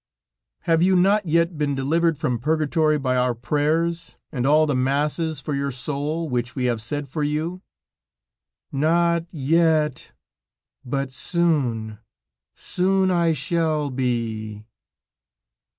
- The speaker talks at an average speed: No, slow, 120 wpm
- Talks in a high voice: No, medium, 150 Hz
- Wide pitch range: No, average, 4.3 semitones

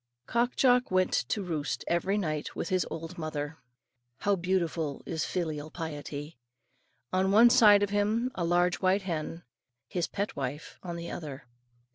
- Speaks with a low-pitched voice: No, medium, 175 Hz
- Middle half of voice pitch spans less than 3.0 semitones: No, average, 4.2 semitones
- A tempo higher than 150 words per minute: Yes, average, 160 wpm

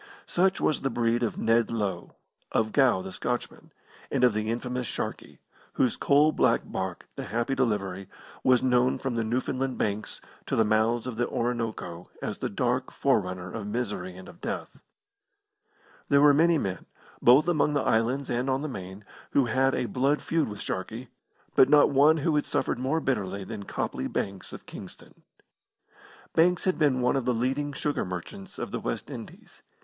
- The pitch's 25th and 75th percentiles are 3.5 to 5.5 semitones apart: Yes, average, 4.4 semitones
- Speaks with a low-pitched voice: Yes, low, 120 Hz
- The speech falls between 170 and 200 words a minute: Yes, average, 180 wpm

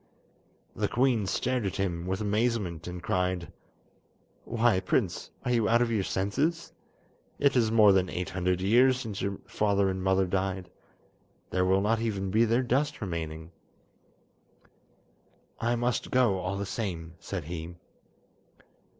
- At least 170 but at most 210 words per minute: No, average, 145 wpm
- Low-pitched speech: Yes, low, 100 Hz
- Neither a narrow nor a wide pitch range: Yes, average, 4.1 semitones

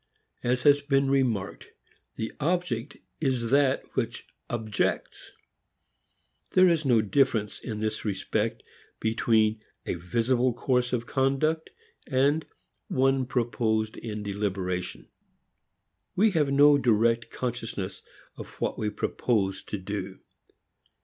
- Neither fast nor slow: No, slow, 110 wpm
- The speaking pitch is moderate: No, low, 120 Hz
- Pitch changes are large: No, average, 4.1 semitones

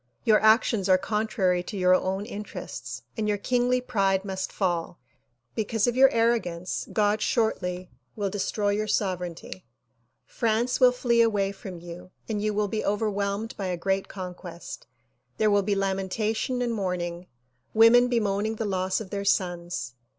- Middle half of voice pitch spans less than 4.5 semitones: Yes, average, 2.9 semitones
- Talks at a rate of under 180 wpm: Yes, average, 155 wpm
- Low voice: No, high, 205 Hz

